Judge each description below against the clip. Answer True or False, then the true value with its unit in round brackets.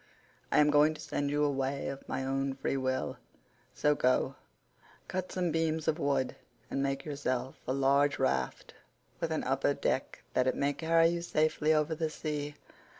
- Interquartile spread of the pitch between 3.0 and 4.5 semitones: False (2.4 semitones)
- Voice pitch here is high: False (145 Hz)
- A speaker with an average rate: True (175 wpm)